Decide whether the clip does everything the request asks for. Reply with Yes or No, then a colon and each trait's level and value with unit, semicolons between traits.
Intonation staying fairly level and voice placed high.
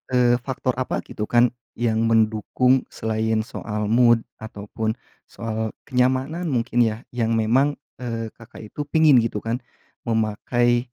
No: narrow, 2.2 semitones; low, 115 Hz